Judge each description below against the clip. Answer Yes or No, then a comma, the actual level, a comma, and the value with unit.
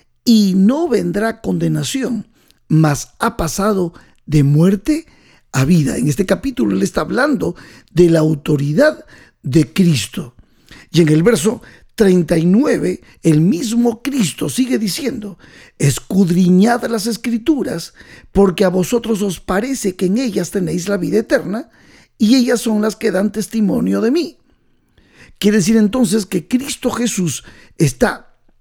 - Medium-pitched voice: No, high, 205 Hz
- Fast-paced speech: No, average, 130 wpm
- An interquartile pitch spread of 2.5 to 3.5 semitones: No, average, 5.3 semitones